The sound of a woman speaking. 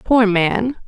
Yes: female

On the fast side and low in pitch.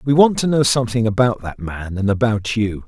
Yes: fast, 210 wpm; low, 115 Hz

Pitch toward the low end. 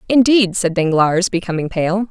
No: high, 190 Hz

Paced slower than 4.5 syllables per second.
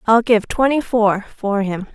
Yes: 4.2 syllables/s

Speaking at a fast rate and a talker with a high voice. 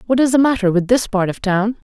Yes: fast, 280 wpm; high, 220 Hz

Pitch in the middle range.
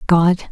Yes: medium, 175 Hz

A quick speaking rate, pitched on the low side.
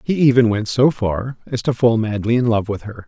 Yes: fast, 255 wpm; low, 115 Hz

